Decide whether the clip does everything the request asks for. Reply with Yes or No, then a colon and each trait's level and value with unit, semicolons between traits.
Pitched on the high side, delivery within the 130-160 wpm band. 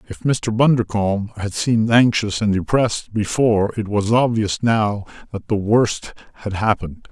No: low, 110 Hz; average, 150 wpm